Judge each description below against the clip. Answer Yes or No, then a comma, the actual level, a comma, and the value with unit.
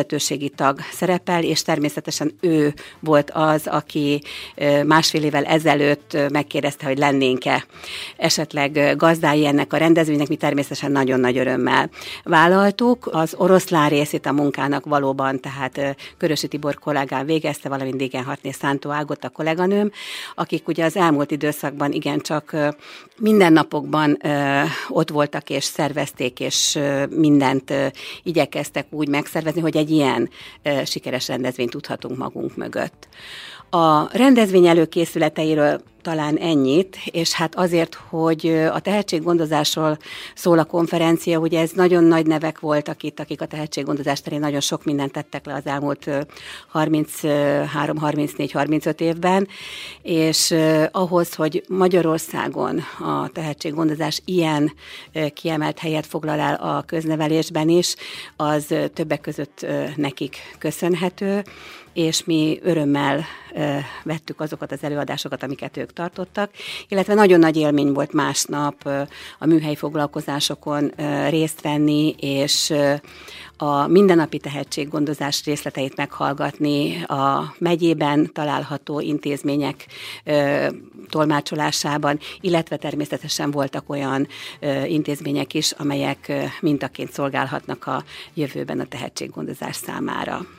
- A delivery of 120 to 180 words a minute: No, average, 110 wpm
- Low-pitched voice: No, medium, 150 Hz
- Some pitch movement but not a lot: No, narrow, 2.2 semitones